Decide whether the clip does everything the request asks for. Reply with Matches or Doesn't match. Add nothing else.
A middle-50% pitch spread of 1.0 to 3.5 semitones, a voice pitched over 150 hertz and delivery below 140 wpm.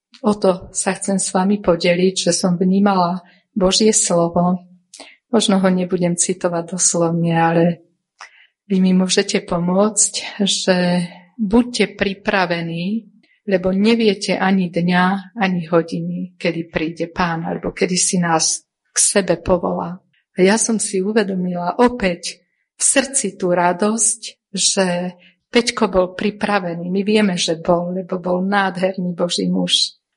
Matches